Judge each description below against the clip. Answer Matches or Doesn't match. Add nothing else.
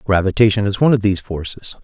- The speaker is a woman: Doesn't match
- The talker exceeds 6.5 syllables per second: Matches